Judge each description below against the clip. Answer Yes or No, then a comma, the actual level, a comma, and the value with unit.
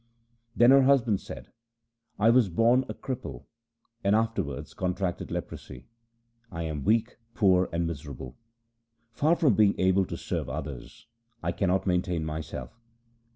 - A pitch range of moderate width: No, wide, 6.1 semitones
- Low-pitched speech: Yes, very low, 95 Hz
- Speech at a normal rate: Yes, average, 145 wpm